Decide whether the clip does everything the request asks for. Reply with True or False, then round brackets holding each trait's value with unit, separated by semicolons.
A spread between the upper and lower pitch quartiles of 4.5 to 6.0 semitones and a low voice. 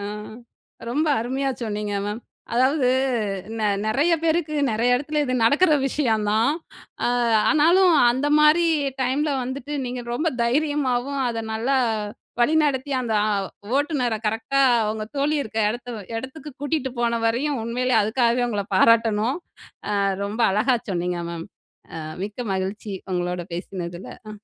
False (4.8 semitones; 245 Hz)